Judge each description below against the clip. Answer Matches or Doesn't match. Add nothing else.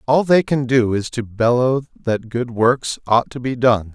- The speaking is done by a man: Matches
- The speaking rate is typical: Doesn't match